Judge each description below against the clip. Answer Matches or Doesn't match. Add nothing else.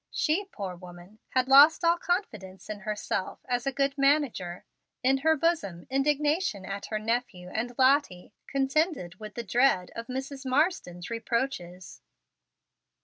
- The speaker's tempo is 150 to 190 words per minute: Doesn't match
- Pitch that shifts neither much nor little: Doesn't match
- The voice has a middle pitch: Doesn't match